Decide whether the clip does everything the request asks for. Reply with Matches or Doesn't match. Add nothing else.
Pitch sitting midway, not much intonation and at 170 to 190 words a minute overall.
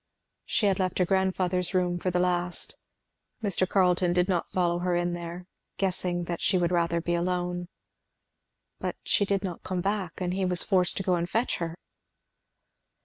Matches